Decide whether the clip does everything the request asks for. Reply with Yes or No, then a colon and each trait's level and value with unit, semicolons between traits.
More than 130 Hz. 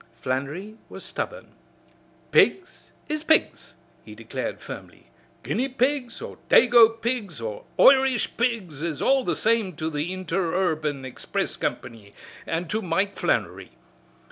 Yes: high, 190 Hz